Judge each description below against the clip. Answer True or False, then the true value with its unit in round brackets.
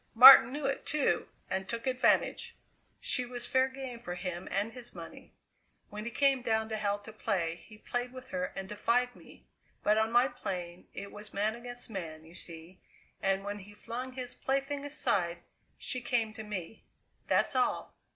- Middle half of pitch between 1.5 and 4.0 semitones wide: False (4.4 semitones)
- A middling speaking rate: True (180 wpm)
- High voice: True (225 Hz)